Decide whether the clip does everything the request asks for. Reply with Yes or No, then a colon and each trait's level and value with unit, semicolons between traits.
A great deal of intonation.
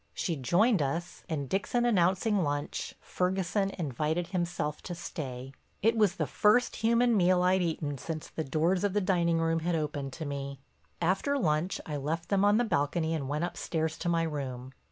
No: average, 4.2 semitones